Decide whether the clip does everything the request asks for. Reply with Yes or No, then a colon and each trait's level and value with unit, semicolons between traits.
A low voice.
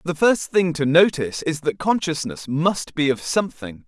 No: medium, 160 Hz